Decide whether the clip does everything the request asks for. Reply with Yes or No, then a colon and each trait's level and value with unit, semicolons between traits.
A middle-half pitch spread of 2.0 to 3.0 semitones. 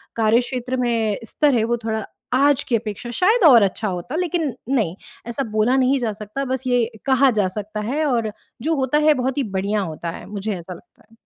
No: average, 4.0 semitones